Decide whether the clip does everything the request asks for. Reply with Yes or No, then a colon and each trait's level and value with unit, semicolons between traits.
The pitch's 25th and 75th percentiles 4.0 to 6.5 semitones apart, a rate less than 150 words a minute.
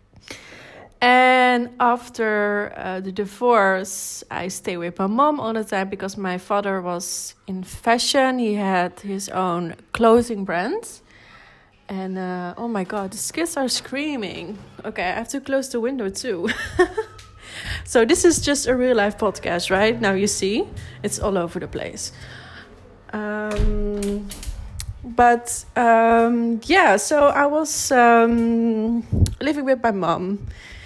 Yes: average, 4.3 semitones; average, 140 wpm